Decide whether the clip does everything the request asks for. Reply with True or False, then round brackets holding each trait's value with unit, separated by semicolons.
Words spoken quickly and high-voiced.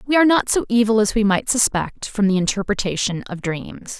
True (210 wpm; 215 Hz)